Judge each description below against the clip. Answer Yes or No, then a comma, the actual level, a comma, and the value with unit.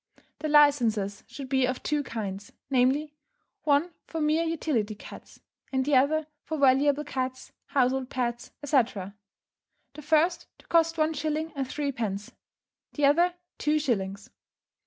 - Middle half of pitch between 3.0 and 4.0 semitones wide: Yes, average, 3.6 semitones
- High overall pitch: Yes, very high, 280 Hz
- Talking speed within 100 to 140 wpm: Yes, slow, 135 wpm